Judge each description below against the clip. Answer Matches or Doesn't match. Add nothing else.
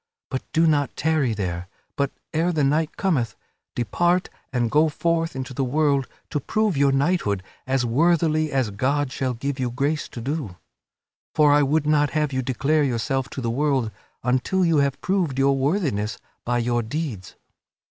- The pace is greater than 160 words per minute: Matches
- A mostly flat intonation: Doesn't match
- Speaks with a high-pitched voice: Doesn't match